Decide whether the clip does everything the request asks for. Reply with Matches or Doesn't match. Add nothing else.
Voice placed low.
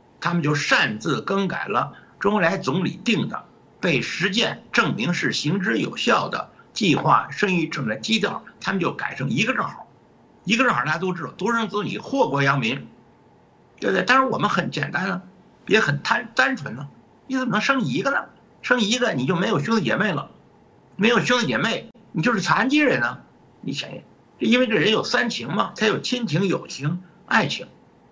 Doesn't match